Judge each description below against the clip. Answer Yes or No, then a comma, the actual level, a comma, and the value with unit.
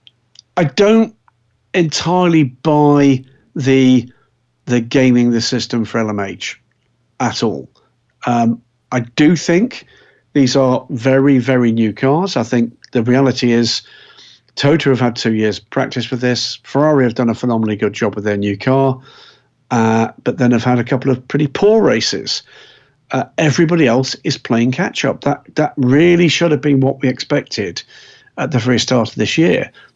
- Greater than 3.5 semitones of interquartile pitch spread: No, average, 3.2 semitones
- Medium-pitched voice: No, low, 125 Hz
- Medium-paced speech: Yes, average, 160 wpm